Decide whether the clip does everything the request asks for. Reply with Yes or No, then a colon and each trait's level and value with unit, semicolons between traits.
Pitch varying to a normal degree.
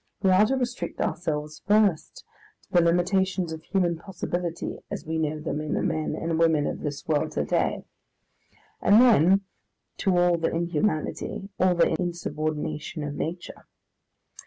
Yes: average, 3.1 semitones